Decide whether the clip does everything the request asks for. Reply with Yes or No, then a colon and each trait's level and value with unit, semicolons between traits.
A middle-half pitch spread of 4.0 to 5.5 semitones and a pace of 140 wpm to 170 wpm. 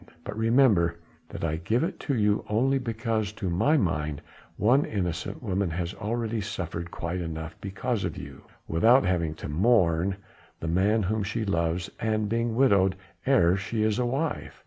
Yes: average, 5.1 semitones; average, 165 wpm